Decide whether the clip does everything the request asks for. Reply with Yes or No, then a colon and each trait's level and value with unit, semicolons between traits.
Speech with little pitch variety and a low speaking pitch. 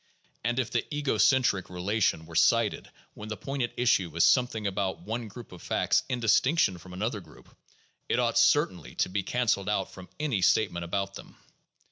No: average, 4.5 semitones; low, 105 Hz